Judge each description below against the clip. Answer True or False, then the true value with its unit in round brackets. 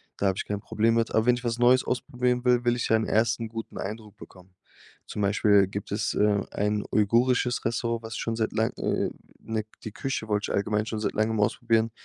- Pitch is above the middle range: False (110 Hz)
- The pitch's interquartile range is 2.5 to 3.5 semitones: False (2.1 semitones)